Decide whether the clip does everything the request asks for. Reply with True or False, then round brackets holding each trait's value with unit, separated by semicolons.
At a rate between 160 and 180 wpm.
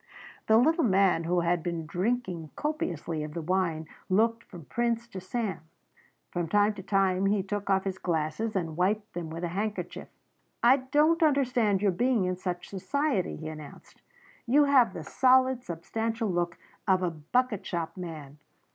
True (165 wpm)